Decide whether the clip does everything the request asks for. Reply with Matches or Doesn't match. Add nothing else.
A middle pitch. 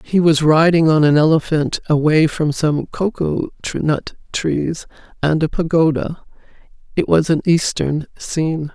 Matches